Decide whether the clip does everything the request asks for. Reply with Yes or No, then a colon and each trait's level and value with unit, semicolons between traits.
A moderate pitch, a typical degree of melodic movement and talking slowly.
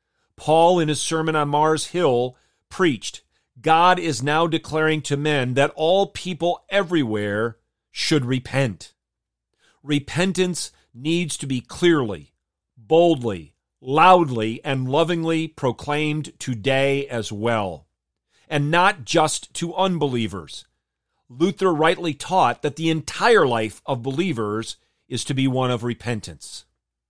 No: medium, 145 Hz; wide, 5.8 semitones; slow, 115 wpm